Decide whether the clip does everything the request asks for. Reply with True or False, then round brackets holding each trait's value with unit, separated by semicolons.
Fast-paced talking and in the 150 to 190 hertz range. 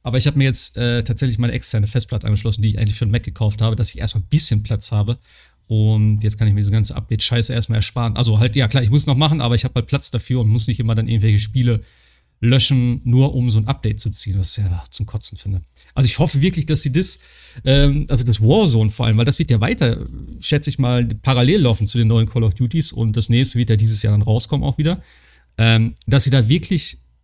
False (260 wpm; 115 Hz)